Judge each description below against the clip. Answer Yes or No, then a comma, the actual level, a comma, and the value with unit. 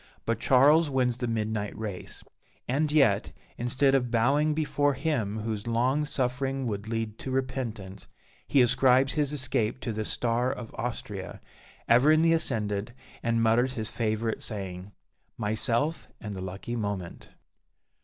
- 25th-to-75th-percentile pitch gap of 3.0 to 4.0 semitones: Yes, average, 3.7 semitones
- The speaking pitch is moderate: No, low, 120 Hz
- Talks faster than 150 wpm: No, average, 145 wpm